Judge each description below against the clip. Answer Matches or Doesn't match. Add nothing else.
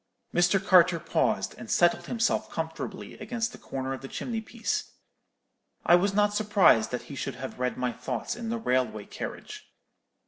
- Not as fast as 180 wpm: Matches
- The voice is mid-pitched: Matches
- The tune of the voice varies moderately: Doesn't match